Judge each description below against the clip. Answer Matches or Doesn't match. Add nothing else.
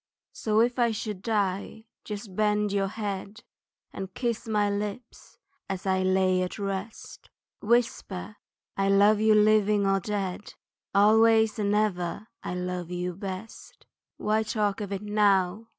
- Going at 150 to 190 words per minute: Doesn't match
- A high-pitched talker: Matches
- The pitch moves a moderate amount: Doesn't match